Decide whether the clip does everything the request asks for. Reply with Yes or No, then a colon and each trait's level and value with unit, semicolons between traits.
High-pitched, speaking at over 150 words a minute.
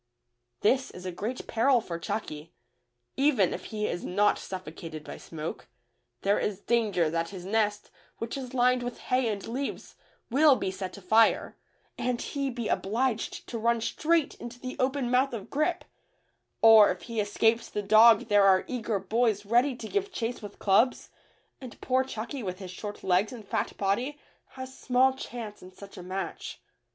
Yes: high, 225 Hz; average, 175 wpm